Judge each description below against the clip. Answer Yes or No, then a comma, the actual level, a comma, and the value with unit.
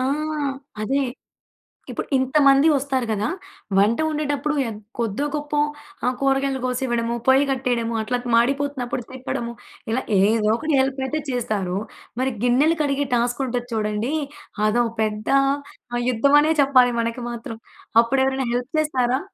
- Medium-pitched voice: No, very high, 255 Hz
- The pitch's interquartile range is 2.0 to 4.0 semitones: Yes, average, 3.0 semitones